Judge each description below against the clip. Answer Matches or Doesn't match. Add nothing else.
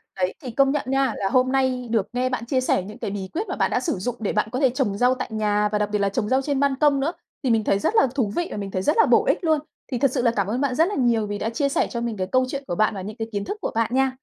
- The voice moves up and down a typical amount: Matches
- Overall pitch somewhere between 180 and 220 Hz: Doesn't match